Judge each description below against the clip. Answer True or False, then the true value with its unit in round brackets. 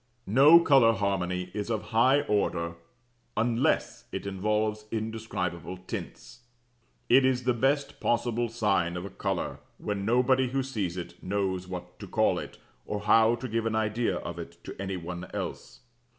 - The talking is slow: False (160 wpm)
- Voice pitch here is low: True (110 Hz)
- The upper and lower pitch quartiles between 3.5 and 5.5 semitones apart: True (4.0 semitones)